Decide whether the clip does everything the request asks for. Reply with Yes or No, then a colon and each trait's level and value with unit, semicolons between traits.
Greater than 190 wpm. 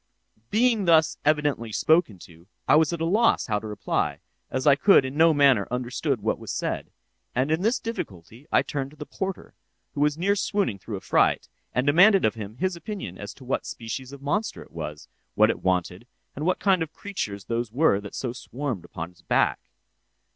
Yes: average, 200 wpm